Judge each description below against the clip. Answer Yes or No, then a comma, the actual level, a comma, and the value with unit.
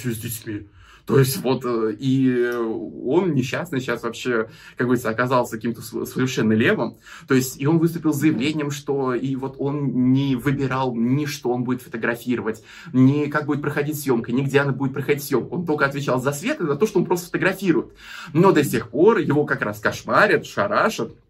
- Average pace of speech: No, fast, 185 wpm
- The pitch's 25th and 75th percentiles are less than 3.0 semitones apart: No, average, 3.4 semitones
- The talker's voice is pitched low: Yes, low, 130 Hz